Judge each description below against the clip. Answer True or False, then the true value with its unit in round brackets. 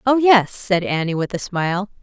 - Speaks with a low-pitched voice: False (195 Hz)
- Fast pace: True (210 wpm)